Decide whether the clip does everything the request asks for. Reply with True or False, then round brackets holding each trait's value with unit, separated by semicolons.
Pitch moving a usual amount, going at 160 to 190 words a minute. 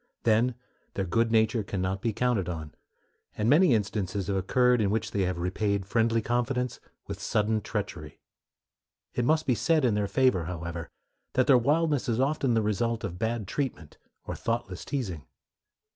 True (4.3 semitones; 170 wpm)